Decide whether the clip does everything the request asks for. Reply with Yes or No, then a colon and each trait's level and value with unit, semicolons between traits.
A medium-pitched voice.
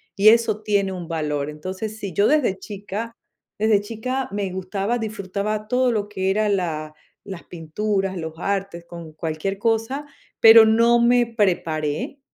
No: high, 200 Hz